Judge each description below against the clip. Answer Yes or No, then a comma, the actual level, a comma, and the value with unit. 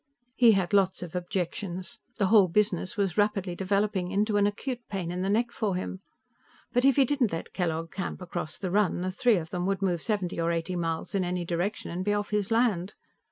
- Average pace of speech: No, fast, 215 wpm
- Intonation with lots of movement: No, average, 2.9 semitones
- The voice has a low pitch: No, high, 190 Hz